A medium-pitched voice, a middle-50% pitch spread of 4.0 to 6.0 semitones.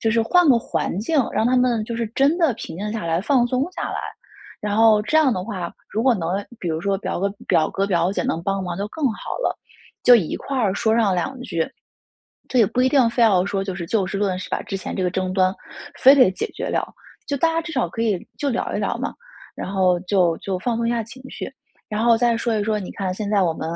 No: high, 210 Hz; average, 4.5 semitones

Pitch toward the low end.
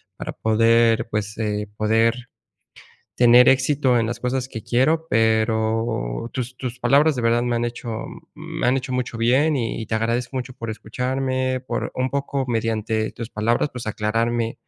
Yes: low, 120 Hz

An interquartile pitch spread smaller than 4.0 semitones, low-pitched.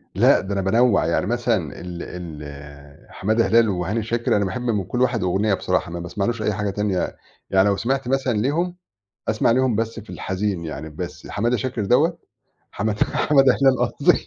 No: average, 4.4 semitones; low, 105 Hz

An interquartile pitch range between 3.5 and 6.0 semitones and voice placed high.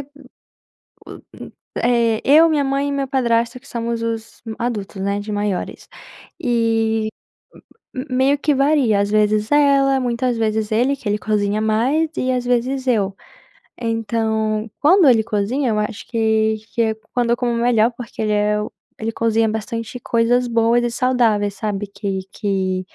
No: average, 2.8 semitones; high, 230 Hz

